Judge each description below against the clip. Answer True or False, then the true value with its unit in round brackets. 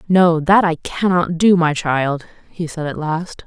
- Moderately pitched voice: True (165 Hz)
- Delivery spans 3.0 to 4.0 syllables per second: True (3.9 syllables/s)